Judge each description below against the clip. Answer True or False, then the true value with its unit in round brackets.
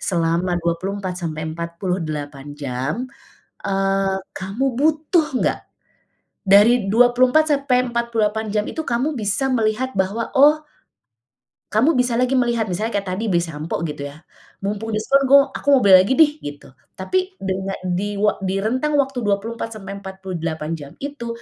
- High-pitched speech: True (205 Hz)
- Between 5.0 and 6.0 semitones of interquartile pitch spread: True (5.4 semitones)